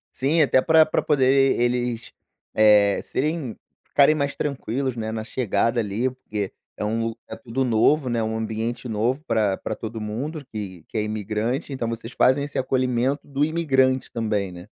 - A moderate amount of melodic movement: Yes, average, 3.7 semitones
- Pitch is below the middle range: Yes, low, 120 Hz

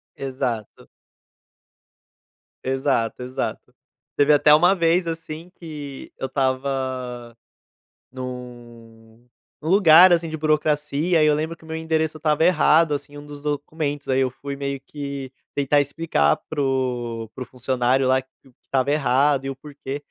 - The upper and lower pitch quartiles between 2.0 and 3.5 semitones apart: Yes, average, 3.0 semitones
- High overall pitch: No, medium, 140 Hz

